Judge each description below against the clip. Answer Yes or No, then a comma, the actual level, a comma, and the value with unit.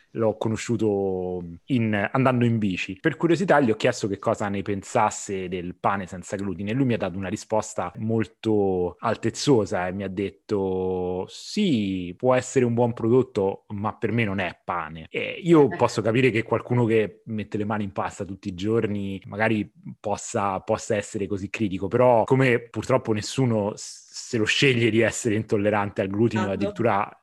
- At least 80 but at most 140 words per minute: No, fast, 170 wpm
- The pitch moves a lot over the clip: No, average, 2.9 semitones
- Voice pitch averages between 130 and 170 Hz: No, low, 105 Hz